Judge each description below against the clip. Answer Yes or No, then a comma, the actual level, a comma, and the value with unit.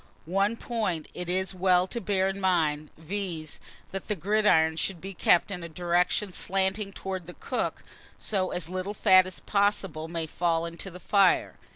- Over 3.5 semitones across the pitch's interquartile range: No, narrow, 2.6 semitones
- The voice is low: No, medium, 185 Hz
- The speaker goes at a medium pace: Yes, average, 180 wpm